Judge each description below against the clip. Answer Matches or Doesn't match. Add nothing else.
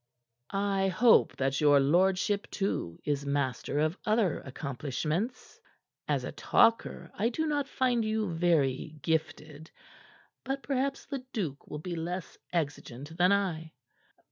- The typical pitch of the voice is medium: Matches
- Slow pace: Matches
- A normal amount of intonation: Doesn't match